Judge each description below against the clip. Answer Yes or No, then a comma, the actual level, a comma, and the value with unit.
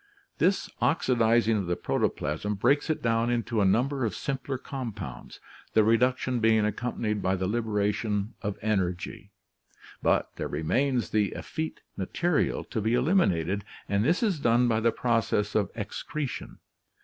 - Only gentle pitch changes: No, average, 3.7 semitones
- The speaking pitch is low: Yes, low, 115 Hz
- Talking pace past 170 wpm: No, average, 145 wpm